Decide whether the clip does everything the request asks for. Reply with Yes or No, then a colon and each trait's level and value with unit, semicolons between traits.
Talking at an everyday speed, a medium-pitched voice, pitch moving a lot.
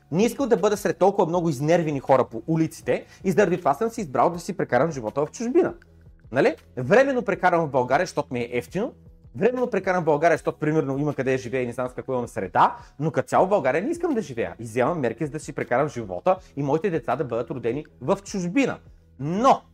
No: fast, 225 wpm; medium, 155 Hz; wide, 7.0 semitones